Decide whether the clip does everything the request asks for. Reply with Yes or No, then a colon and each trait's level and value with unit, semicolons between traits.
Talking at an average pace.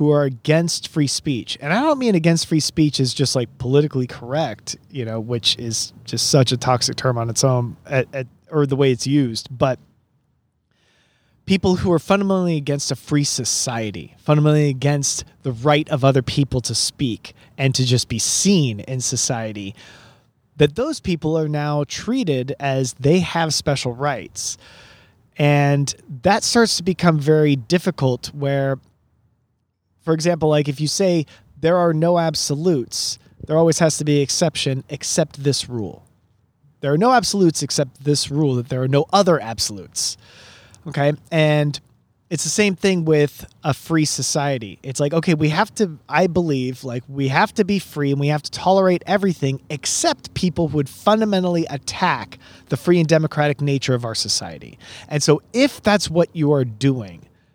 Yes: average, 170 wpm